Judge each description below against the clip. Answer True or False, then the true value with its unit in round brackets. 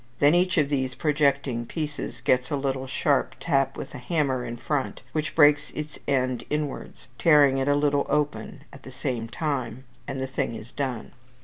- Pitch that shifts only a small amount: True (2.3 semitones)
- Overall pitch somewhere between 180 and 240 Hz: False (140 Hz)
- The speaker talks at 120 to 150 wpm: False (190 wpm)